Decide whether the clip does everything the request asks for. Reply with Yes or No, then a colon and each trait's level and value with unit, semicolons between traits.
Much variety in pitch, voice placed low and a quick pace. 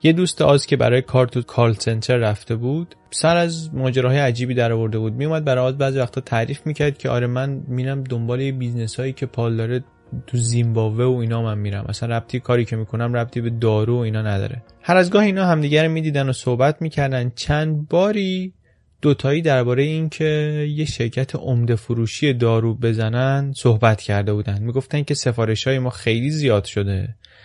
No: average, 3.8 semitones; low, 125 Hz; fast, 190 wpm